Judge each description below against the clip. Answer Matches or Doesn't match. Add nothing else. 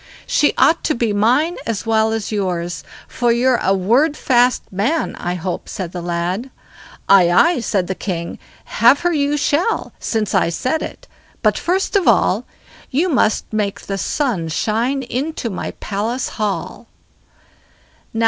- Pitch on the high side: Matches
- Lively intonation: Matches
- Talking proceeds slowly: Doesn't match